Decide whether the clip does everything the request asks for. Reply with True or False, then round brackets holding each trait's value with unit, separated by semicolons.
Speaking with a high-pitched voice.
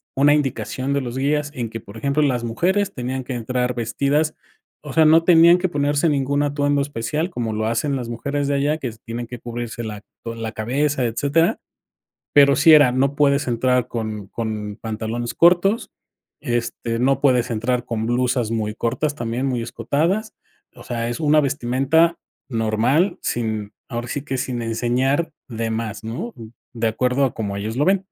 False (125 Hz)